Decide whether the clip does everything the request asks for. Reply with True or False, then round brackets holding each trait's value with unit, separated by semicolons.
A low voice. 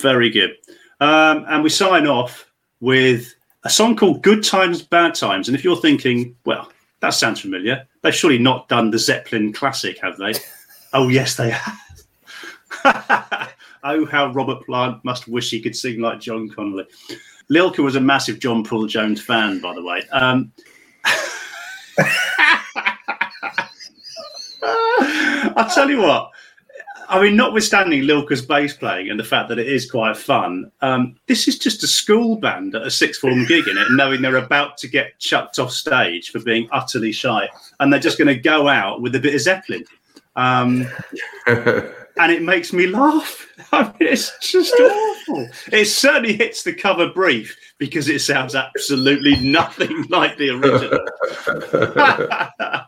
False (145 Hz)